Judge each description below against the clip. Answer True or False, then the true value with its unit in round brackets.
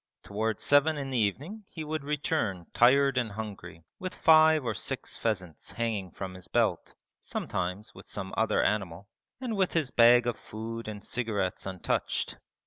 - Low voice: True (115 Hz)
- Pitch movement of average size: False (6.4 semitones)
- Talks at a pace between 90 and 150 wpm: False (160 wpm)